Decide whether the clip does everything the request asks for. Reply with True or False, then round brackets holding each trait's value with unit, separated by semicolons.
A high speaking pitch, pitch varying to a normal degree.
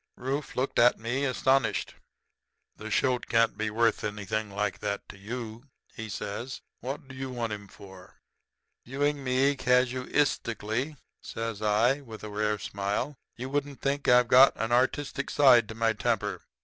False (120 Hz; 3.8 semitones)